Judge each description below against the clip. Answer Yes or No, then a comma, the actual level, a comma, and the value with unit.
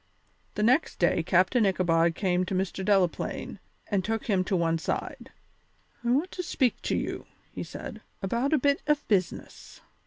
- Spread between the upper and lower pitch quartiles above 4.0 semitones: Yes, average, 5.2 semitones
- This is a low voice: No, high, 195 Hz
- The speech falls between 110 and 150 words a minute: No, average, 165 wpm